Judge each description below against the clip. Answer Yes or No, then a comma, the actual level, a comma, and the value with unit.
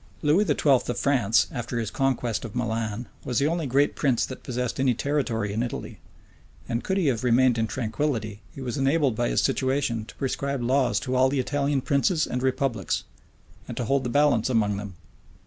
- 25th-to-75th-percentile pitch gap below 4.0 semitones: Yes, average, 3.2 semitones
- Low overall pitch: Yes, low, 130 Hz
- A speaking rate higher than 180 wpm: Yes, average, 195 wpm